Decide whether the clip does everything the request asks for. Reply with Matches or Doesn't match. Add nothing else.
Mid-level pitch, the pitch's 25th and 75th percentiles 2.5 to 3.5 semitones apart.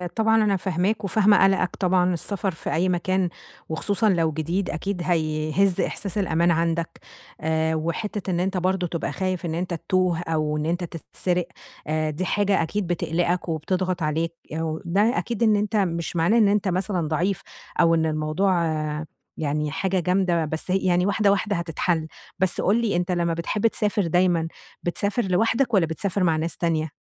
Matches